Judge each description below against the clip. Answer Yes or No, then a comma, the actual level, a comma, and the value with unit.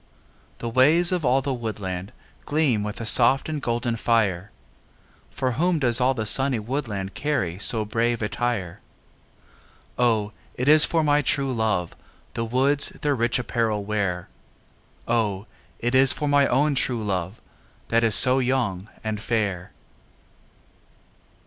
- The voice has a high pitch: No, low, 120 Hz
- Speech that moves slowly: No, average, 145 wpm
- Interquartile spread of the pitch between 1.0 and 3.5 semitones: No, average, 4.1 semitones